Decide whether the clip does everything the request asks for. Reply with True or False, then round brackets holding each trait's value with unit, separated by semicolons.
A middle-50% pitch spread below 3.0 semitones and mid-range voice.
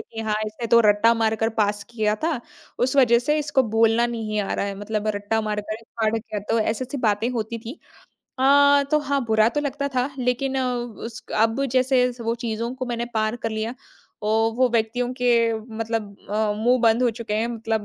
False (2.4 semitones; 230 Hz)